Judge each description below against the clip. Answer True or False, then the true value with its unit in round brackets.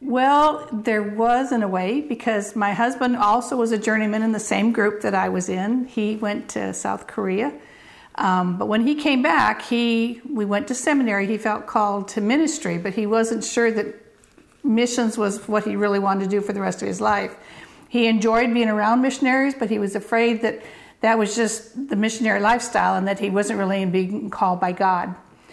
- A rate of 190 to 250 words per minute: True (200 wpm)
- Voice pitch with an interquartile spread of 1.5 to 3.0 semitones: True (2.7 semitones)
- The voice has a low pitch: False (220 Hz)